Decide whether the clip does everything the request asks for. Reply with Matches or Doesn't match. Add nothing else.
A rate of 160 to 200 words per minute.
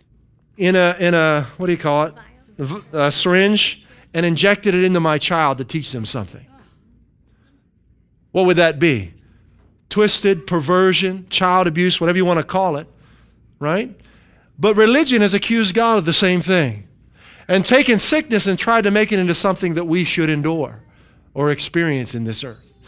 Matches